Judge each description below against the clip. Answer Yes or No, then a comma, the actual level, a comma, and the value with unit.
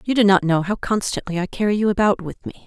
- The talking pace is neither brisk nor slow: No, fast, 270 wpm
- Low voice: No, high, 195 Hz